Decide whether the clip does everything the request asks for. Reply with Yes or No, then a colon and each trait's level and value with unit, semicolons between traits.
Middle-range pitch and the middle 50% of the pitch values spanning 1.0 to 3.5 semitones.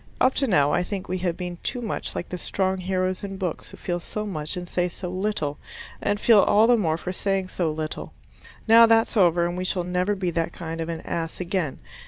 Yes: medium, 180 Hz; average, 2.7 semitones